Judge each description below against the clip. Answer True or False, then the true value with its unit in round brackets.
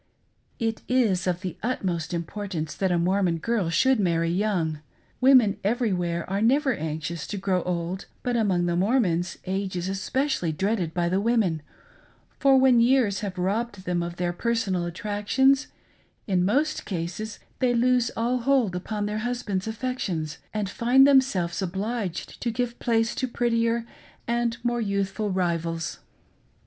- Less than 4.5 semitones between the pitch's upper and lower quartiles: False (5.1 semitones)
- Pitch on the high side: True (200 Hz)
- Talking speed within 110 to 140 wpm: False (150 wpm)